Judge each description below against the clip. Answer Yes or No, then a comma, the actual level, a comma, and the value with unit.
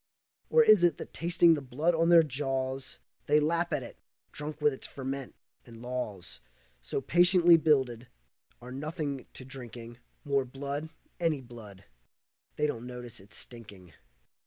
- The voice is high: No, low, 135 Hz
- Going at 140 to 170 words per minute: Yes, average, 150 wpm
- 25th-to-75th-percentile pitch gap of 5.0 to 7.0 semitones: No, average, 4.3 semitones